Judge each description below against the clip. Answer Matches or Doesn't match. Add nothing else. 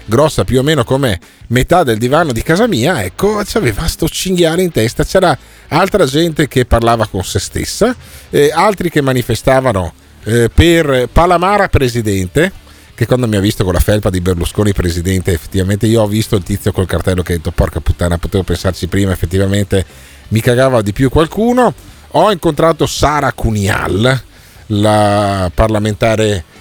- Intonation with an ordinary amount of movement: Doesn't match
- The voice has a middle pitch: Doesn't match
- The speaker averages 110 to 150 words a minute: Doesn't match